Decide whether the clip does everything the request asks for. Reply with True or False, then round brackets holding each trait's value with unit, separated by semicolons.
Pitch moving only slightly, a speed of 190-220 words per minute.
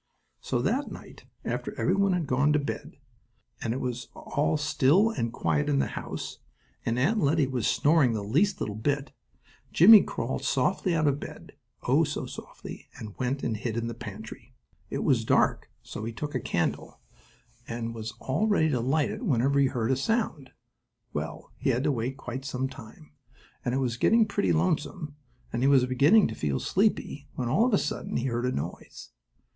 False (4.6 semitones; 195 wpm)